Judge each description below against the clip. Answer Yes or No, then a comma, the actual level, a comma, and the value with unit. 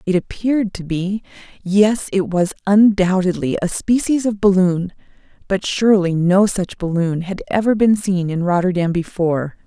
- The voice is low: No, high, 190 Hz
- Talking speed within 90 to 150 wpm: Yes, average, 145 wpm